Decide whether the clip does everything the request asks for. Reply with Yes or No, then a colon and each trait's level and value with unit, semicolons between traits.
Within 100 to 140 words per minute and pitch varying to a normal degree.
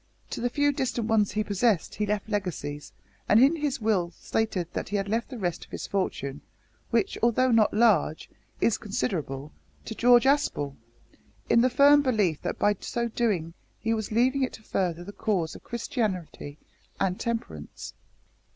No: average, 170 wpm; average, 4.9 semitones